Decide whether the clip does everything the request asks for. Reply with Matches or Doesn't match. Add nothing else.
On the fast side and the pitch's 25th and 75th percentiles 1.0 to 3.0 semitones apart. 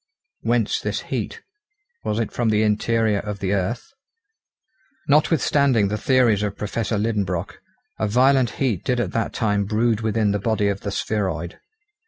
Doesn't match